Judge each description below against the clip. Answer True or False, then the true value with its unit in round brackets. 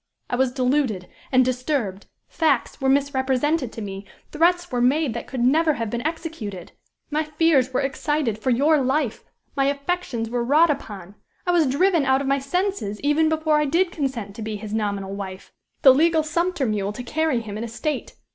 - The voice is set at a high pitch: True (270 Hz)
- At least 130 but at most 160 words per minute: False (185 wpm)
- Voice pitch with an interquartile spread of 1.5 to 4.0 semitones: False (5.2 semitones)